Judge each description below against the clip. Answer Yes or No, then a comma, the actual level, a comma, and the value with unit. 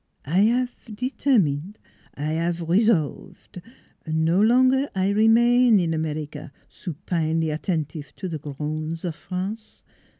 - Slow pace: Yes, slow, 120 wpm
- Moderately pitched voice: Yes, medium, 175 Hz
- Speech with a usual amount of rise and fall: No, wide, 5.8 semitones